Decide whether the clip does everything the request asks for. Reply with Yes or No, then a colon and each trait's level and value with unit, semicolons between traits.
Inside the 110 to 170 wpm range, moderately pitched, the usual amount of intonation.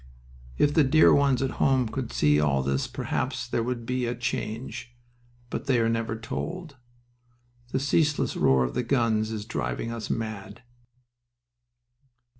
No: average, 150 wpm; low, 115 Hz; average, 3.6 semitones